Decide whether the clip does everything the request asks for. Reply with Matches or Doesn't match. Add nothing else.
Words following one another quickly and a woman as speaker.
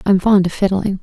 Matches